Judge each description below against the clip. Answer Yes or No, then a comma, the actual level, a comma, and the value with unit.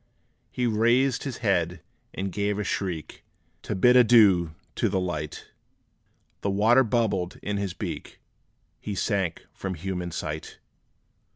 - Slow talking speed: Yes, slow, 125 wpm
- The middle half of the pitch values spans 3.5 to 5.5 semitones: Yes, average, 4.1 semitones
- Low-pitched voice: Yes, low, 100 Hz